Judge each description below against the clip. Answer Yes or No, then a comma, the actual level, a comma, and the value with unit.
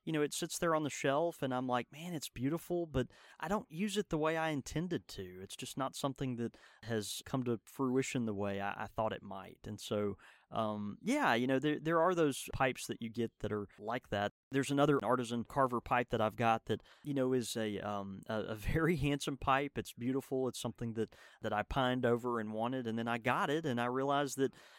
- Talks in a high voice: No, low, 125 Hz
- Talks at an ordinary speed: No, fast, 235 wpm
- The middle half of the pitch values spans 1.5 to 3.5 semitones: No, average, 4.2 semitones